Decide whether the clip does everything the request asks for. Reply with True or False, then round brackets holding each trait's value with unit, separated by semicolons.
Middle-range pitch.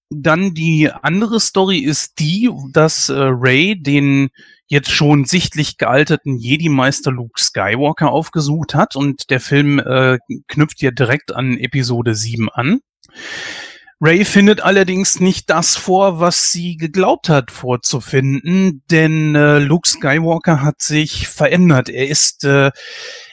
True (150 Hz)